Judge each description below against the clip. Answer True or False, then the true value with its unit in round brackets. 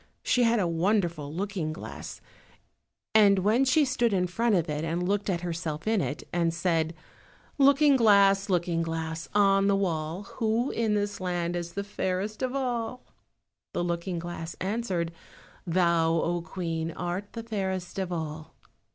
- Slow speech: False (160 wpm)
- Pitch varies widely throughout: False (3.9 semitones)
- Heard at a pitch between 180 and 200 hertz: True (185 Hz)